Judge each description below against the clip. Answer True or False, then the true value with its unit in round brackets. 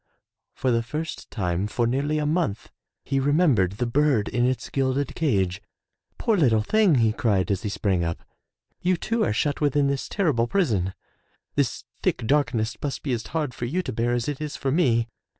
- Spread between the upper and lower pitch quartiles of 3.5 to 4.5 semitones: False (5.2 semitones)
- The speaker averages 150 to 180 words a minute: False (190 wpm)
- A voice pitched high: False (130 Hz)